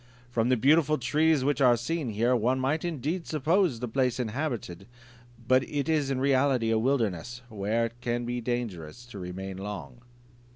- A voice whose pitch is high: No, low, 125 Hz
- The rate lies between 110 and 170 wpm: Yes, average, 165 wpm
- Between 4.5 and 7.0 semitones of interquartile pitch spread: No, average, 3.8 semitones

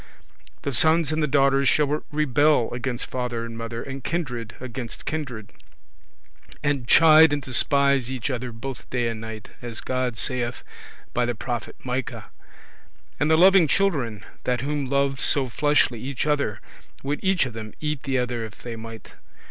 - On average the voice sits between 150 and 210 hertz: No, low, 130 Hz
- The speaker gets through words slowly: No, average, 165 wpm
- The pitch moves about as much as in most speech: Yes, average, 3.6 semitones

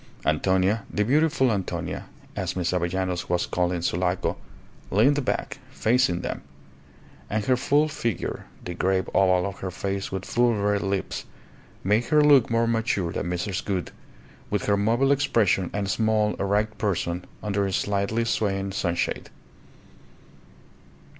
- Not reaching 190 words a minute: Yes, average, 140 wpm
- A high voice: No, low, 100 Hz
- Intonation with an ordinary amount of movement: Yes, average, 3.7 semitones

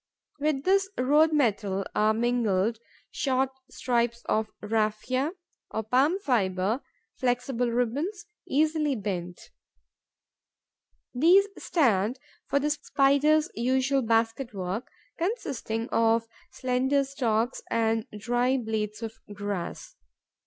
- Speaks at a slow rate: Yes, slow, 100 wpm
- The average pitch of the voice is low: No, high, 245 Hz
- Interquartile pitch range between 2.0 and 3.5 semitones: No, average, 4.1 semitones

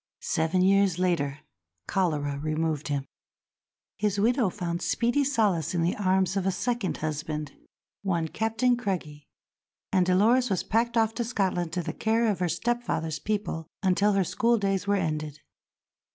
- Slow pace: No, average, 150 wpm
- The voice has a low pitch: No, high, 190 Hz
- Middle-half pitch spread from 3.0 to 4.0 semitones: No, average, 5.2 semitones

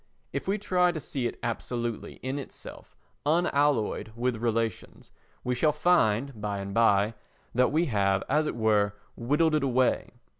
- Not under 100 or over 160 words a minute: Yes, average, 155 wpm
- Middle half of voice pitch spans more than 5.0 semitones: Yes, wide, 5.4 semitones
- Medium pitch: No, low, 125 Hz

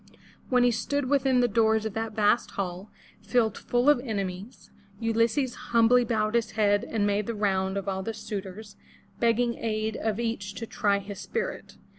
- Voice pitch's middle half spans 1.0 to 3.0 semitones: Yes, average, 2.7 semitones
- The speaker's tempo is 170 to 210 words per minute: Yes, average, 175 wpm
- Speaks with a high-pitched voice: Yes, high, 220 Hz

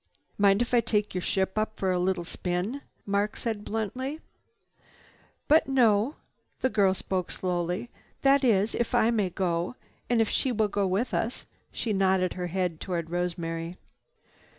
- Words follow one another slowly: No, average, 160 wpm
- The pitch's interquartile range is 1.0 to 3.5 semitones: No, average, 4.0 semitones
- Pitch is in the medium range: No, high, 200 Hz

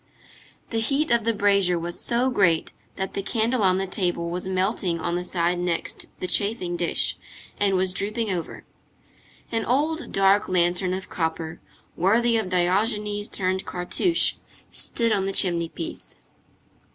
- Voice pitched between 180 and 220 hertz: Yes, high, 190 Hz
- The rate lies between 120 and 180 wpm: Yes, average, 150 wpm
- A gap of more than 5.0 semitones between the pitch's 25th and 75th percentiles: No, average, 3.7 semitones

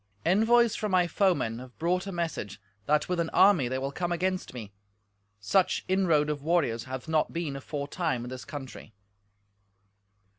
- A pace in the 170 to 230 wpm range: No, average, 160 wpm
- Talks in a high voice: No, medium, 160 Hz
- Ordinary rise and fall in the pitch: No, wide, 5.7 semitones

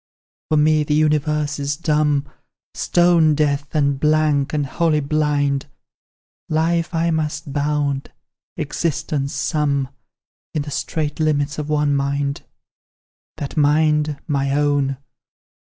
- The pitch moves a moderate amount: No, narrow, 1.4 semitones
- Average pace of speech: No, slow, 115 wpm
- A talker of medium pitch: Yes, medium, 150 Hz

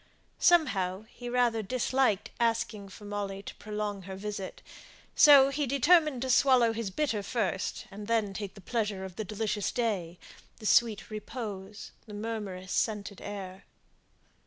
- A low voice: No, high, 215 Hz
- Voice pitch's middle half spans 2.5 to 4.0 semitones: Yes, average, 3.3 semitones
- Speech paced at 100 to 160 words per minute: Yes, average, 145 wpm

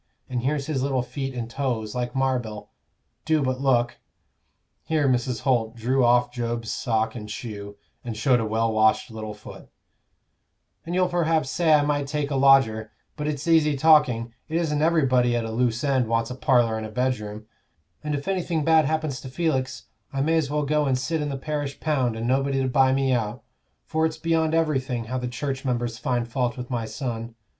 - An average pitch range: Yes, average, 4.0 semitones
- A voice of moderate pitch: No, low, 130 Hz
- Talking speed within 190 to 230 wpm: Yes, average, 200 wpm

